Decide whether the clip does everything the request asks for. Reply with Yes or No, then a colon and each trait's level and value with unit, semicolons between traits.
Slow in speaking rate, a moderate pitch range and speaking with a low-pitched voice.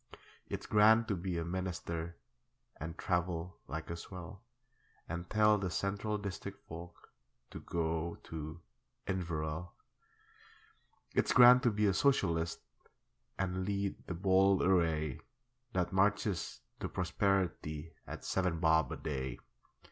Yes: slow, 125 wpm; average, 3.1 semitones; very low, 90 Hz